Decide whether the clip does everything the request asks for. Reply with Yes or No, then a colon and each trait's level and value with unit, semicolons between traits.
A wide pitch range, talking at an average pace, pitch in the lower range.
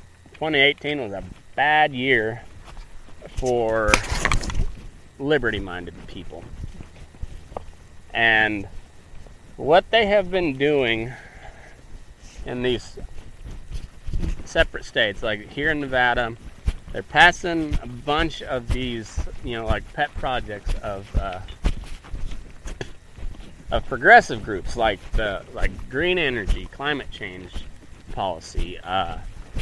No: wide, 6.7 semitones; slow, 95 wpm; low, 110 Hz